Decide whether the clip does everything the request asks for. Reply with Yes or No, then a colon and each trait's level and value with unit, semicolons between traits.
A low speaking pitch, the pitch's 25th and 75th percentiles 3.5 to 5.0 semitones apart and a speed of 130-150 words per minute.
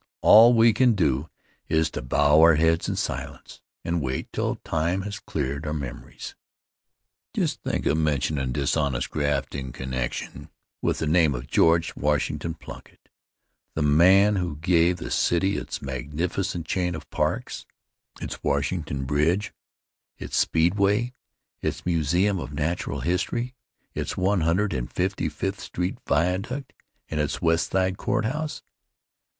Yes: very low, 80 Hz; average, 4.4 semitones; average, 140 wpm